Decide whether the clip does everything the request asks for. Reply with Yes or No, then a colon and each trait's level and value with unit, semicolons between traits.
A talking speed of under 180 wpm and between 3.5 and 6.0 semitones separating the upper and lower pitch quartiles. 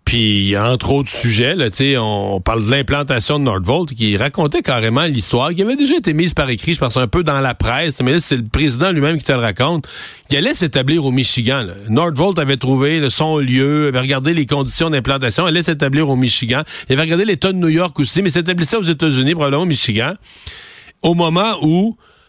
No: average, 210 wpm; average, 4.8 semitones